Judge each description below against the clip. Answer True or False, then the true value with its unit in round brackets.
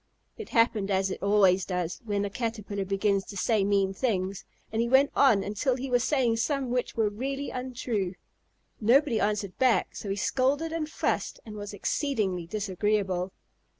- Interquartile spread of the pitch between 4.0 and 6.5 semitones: True (4.3 semitones)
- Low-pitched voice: False (210 Hz)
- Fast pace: False (170 wpm)